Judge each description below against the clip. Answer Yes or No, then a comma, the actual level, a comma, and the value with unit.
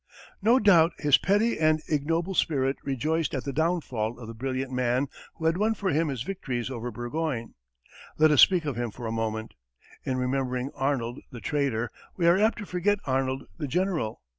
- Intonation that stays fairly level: No, average, 5.1 semitones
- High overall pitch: No, medium, 140 Hz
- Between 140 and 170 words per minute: No, average, 190 wpm